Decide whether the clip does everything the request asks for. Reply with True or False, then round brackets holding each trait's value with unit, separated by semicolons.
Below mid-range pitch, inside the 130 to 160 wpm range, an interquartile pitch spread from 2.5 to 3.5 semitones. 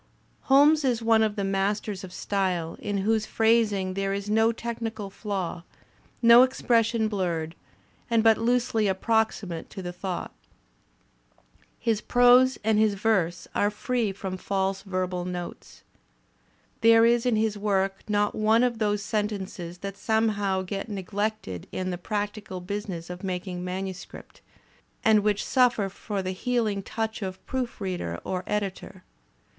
False (205 Hz; 140 wpm; 2.9 semitones)